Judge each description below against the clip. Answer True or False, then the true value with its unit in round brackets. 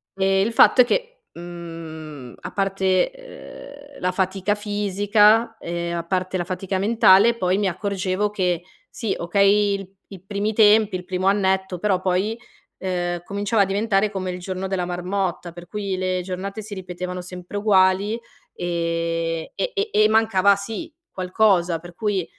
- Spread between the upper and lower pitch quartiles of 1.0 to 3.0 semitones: True (2.5 semitones)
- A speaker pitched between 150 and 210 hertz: True (190 Hz)